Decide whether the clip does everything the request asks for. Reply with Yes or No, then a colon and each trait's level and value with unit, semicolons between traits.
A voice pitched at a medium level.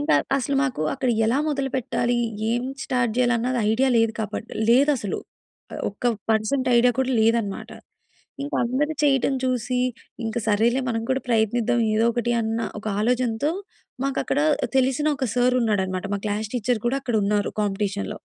No: high, 240 Hz